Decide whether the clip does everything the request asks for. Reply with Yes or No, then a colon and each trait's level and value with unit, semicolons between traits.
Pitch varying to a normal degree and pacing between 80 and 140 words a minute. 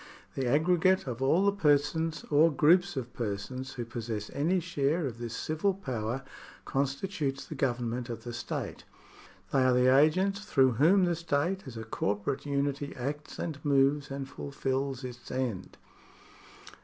No: average, 4.1 semitones; average, 155 wpm